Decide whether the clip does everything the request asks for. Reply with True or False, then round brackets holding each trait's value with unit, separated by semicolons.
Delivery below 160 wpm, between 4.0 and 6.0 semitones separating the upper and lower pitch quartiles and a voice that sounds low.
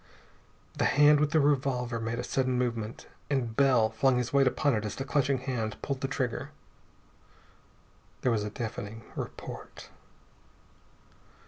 False (145 wpm; 3.3 semitones; 125 Hz)